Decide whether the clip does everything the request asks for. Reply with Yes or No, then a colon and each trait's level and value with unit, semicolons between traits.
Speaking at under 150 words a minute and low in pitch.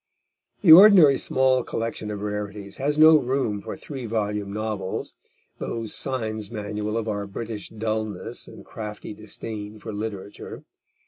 Yes: slow, 135 wpm; low, 110 Hz